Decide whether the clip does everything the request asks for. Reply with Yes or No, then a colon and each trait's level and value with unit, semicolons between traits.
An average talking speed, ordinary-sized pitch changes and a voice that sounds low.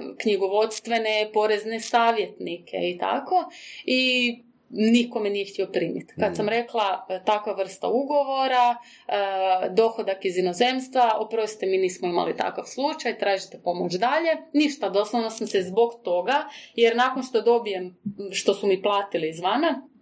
No: average, 135 wpm; average, 3.9 semitones; high, 220 Hz